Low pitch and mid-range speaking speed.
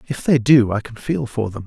No: low, 120 Hz; fast, 290 wpm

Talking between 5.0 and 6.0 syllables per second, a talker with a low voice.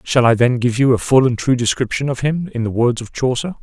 Yes: 5.7 syllables/s; low, 125 Hz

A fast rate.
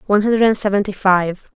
No: average, 155 wpm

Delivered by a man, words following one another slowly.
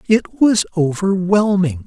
Yes: male; slow, 95 wpm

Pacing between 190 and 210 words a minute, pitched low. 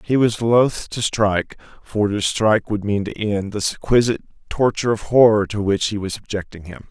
Yes: average, 200 wpm; low, 105 Hz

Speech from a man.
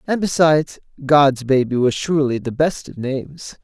Yes: male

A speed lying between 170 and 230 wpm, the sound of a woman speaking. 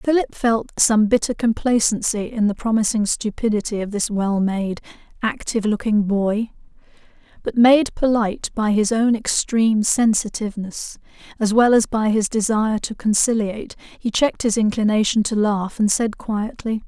No: average, 145 wpm; female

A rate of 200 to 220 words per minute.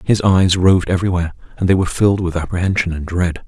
Yes: fast, 205 wpm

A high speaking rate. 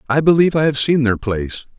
Yes: fast, 235 wpm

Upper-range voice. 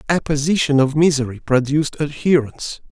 No: medium, 145 Hz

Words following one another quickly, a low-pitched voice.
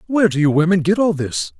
No: fast, 265 wpm; medium, 165 Hz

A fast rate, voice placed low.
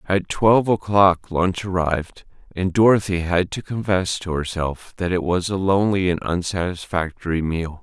No: average, 155 wpm; very low, 90 Hz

